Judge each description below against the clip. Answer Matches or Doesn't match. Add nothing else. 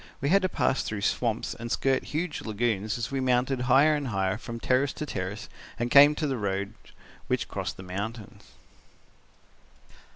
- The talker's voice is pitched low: Matches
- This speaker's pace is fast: Doesn't match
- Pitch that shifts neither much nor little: Matches